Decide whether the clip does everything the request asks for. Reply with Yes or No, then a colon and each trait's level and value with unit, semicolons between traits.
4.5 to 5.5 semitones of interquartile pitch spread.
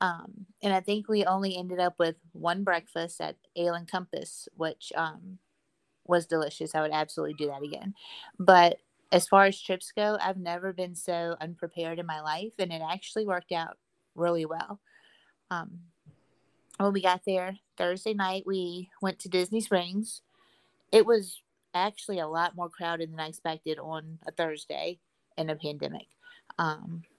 No: narrow, 2.6 semitones